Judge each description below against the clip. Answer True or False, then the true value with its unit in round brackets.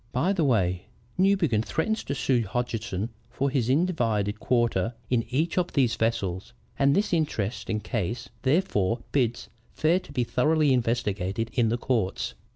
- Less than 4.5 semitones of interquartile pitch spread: False (4.8 semitones)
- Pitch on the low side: True (120 Hz)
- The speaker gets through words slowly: False (150 wpm)